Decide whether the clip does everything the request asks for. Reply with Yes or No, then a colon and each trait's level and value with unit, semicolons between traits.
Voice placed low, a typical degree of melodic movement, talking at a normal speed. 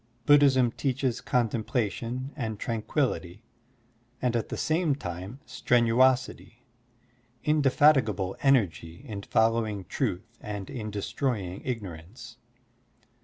No: low, 115 Hz; average, 4.2 semitones; slow, 100 wpm